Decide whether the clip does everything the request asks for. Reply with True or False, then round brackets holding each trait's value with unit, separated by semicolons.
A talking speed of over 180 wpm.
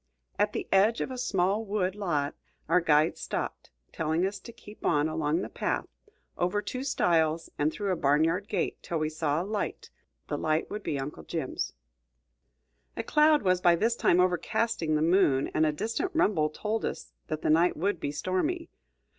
True (190 wpm)